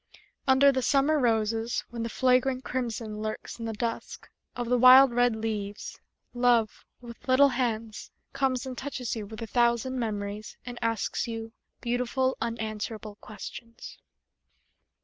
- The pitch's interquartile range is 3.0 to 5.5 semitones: No, narrow, 2.5 semitones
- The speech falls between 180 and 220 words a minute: No, average, 140 wpm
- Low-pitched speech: No, high, 235 Hz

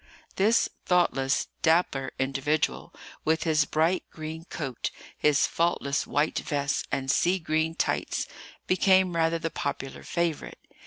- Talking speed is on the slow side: Yes, slow, 120 wpm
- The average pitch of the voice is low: No, medium, 160 Hz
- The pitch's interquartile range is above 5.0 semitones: No, average, 3.2 semitones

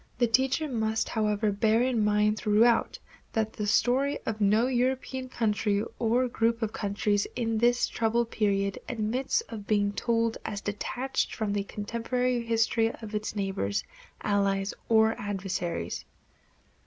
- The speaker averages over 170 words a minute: No, average, 140 wpm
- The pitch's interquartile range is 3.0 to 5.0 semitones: No, narrow, 2.4 semitones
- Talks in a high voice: Yes, high, 220 Hz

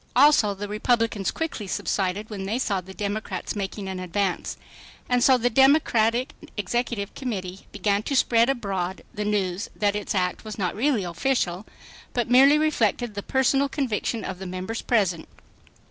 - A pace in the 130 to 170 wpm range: Yes, average, 160 wpm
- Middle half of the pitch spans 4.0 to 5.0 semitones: Yes, average, 4.3 semitones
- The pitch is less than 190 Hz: No, high, 210 Hz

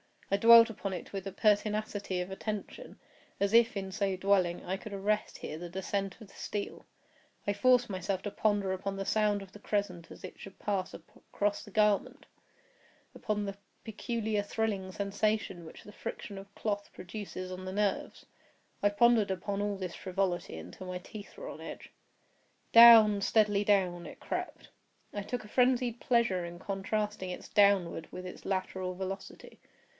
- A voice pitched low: No, high, 200 Hz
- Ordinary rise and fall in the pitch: No, narrow, 2.1 semitones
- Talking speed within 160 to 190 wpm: Yes, average, 165 wpm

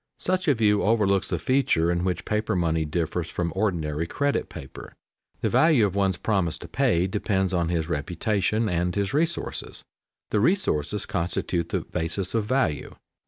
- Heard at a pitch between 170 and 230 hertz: No, very low, 95 Hz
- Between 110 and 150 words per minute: No, average, 165 wpm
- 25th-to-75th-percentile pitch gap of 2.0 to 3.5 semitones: No, average, 4.3 semitones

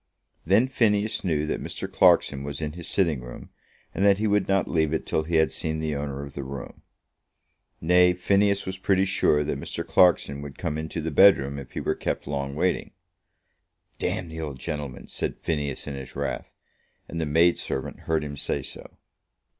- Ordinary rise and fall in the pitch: Yes, average, 4.4 semitones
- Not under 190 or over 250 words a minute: Yes, average, 195 wpm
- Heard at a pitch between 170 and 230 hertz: No, very low, 80 Hz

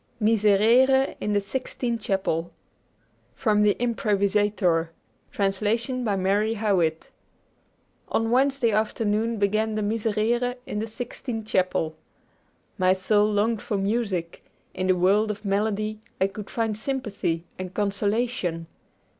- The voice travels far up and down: No, narrow, 2.6 semitones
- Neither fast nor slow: No, slow, 120 wpm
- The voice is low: No, high, 210 Hz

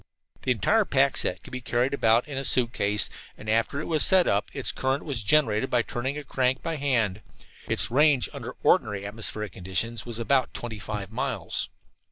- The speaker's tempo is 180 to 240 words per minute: Yes, average, 190 wpm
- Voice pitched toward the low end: Yes, low, 120 Hz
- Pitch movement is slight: No, average, 4.3 semitones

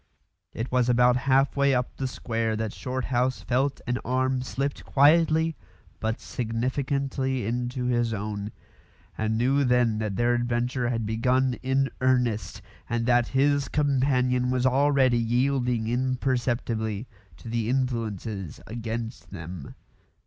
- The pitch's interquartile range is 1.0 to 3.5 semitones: Yes, narrow, 2.4 semitones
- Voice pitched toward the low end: Yes, low, 125 Hz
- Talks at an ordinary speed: No, slow, 125 wpm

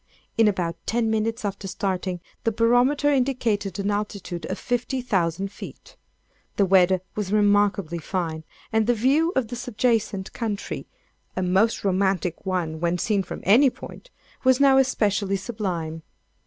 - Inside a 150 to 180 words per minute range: No, slow, 135 wpm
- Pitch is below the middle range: No, high, 205 Hz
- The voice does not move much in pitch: No, average, 4.0 semitones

